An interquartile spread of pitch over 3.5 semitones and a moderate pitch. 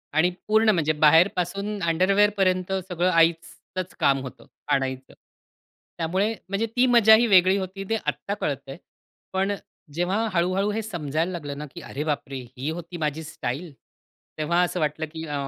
Yes: average, 4.2 semitones; medium, 175 Hz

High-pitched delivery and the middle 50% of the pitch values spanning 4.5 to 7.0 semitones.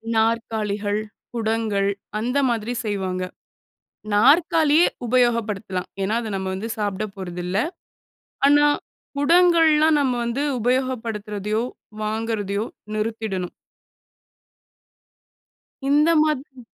No: high, 225 Hz; average, 4.1 semitones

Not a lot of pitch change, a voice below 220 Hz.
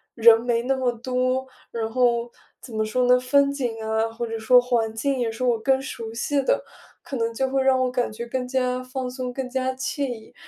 No: narrow, 2.1 semitones; very high, 250 Hz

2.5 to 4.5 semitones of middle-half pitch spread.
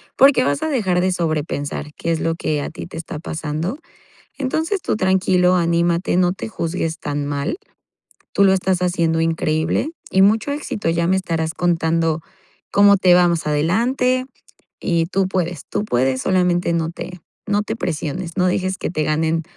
Yes: average, 2.8 semitones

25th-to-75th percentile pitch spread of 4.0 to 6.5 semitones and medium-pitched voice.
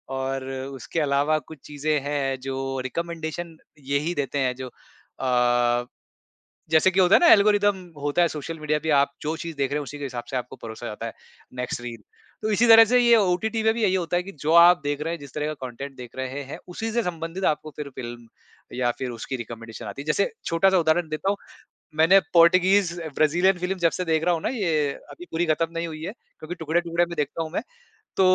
Yes: average, 4.5 semitones; medium, 155 Hz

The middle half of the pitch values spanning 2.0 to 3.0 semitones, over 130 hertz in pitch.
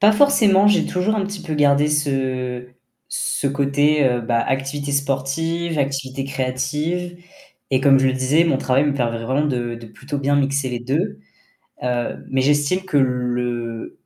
Yes: average, 2.7 semitones; medium, 140 Hz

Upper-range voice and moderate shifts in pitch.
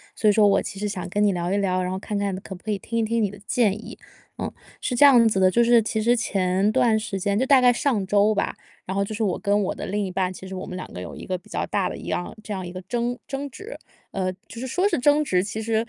Yes: high, 205 Hz; average, 3.5 semitones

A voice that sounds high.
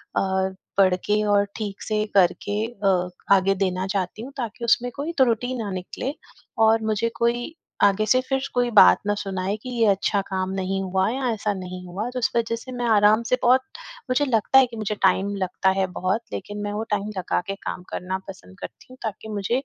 Yes: high, 205 Hz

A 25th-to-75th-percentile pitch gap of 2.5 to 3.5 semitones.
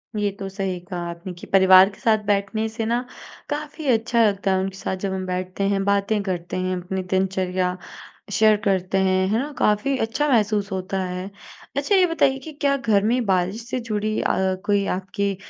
Yes: average, 3.0 semitones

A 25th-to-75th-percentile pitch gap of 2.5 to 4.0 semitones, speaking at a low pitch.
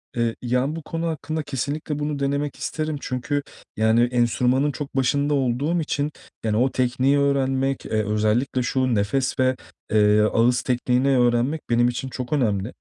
Yes: average, 3.0 semitones; low, 130 Hz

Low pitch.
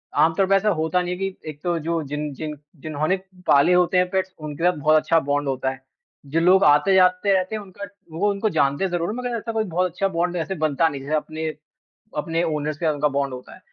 No: medium, 165 Hz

